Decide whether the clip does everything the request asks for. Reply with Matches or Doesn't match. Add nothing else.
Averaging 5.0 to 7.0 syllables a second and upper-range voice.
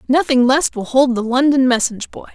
Matches